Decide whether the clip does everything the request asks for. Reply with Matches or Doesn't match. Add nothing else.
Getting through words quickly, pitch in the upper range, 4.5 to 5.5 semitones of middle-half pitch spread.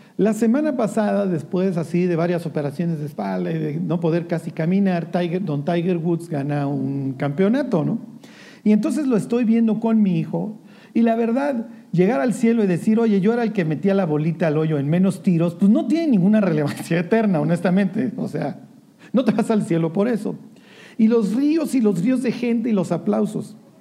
Matches